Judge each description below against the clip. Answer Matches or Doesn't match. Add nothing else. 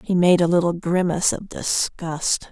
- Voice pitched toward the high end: Doesn't match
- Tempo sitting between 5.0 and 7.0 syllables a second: Doesn't match